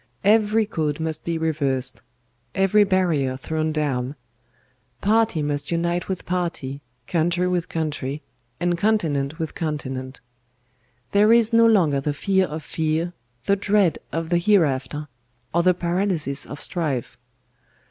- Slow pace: Yes, slow, 130 wpm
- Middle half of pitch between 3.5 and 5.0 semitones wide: Yes, average, 4.2 semitones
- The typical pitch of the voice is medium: Yes, medium, 165 Hz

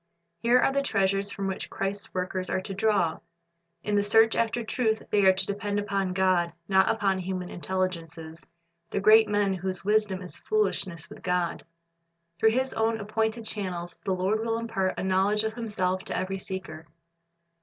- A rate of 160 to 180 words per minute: Yes, average, 175 wpm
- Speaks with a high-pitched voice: Yes, high, 195 Hz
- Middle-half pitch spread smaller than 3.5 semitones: Yes, average, 2.8 semitones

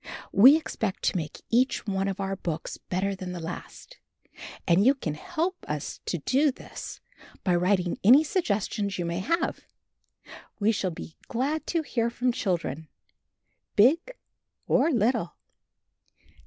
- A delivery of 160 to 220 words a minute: No, average, 140 wpm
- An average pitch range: No, wide, 6.7 semitones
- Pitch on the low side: No, high, 205 Hz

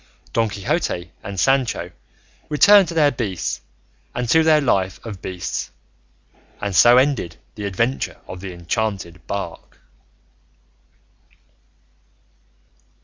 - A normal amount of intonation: No, wide, 6.5 semitones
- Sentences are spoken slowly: Yes, slow, 105 wpm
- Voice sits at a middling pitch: No, low, 105 Hz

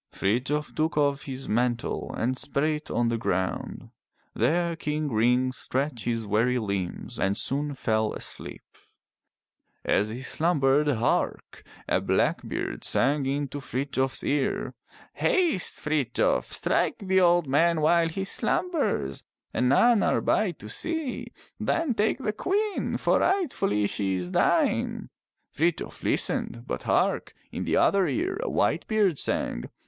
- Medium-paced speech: Yes, average, 145 wpm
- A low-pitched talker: No, medium, 145 Hz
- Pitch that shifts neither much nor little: No, wide, 6.6 semitones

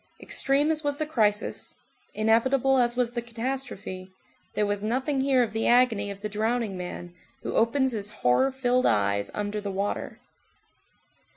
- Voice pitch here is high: Yes, high, 230 Hz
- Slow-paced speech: No, average, 160 wpm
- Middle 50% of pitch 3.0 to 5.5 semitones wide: Yes, average, 4.3 semitones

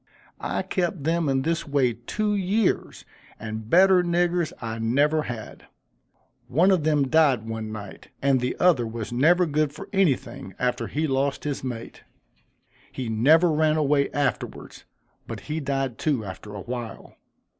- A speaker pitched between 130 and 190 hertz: Yes, medium, 140 Hz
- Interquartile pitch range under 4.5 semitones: No, average, 5.2 semitones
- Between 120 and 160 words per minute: Yes, average, 155 wpm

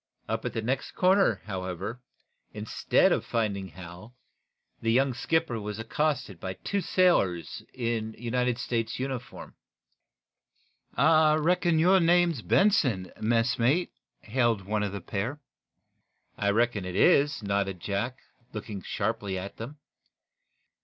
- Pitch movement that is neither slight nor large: No, wide, 6.1 semitones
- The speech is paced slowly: Yes, slow, 125 wpm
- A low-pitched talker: Yes, low, 115 Hz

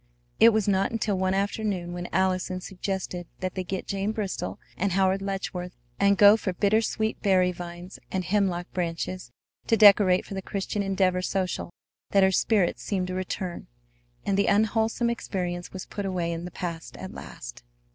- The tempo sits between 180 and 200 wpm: No, average, 170 wpm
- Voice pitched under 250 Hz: Yes, high, 190 Hz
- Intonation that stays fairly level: Yes, narrow, 1.8 semitones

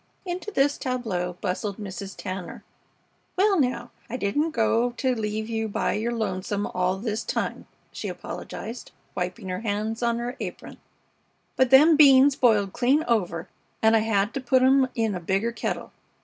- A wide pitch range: No, average, 4.3 semitones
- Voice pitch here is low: No, high, 225 Hz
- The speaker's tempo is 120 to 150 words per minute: No, average, 165 wpm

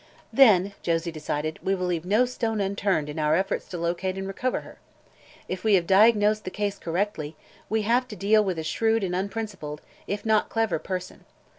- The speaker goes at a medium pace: Yes, average, 190 wpm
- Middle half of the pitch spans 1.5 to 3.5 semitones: No, average, 3.9 semitones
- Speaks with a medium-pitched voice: No, high, 195 Hz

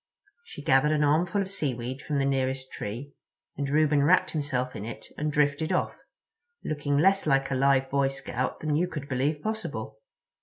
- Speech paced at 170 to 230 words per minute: Yes, average, 175 wpm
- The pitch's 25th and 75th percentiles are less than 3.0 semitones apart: Yes, narrow, 2.6 semitones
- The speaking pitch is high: No, medium, 145 Hz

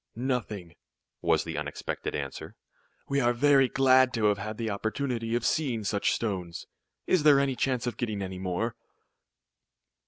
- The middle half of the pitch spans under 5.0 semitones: Yes, average, 4.1 semitones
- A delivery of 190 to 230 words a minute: No, average, 155 wpm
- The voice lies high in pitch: No, low, 115 Hz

